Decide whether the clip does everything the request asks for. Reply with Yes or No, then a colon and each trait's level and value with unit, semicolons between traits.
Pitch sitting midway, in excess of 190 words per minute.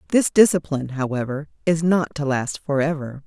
No: medium, 150 Hz; average, 145 wpm